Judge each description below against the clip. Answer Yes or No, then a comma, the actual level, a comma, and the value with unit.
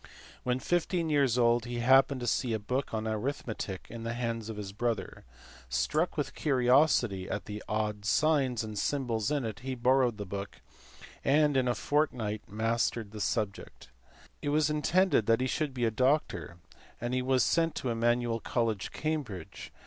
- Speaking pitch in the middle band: No, low, 120 Hz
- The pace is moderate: Yes, average, 175 wpm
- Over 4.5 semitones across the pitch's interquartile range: No, average, 3.9 semitones